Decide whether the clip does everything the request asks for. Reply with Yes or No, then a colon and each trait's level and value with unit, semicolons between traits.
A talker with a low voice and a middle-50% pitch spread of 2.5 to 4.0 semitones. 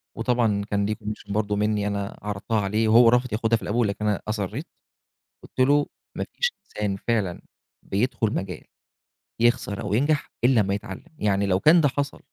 Yes: low, 105 Hz; average, 3.0 semitones